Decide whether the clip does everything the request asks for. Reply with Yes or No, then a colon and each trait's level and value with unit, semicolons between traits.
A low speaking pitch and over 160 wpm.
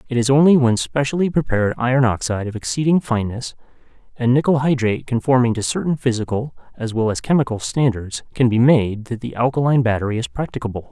Yes: low, 125 Hz; average, 175 wpm